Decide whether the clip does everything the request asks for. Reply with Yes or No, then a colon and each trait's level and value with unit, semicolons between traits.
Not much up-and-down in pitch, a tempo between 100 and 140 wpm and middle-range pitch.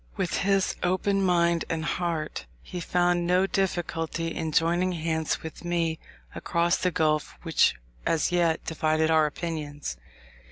Yes: narrow, 1.9 semitones; slow, 135 wpm; medium, 170 Hz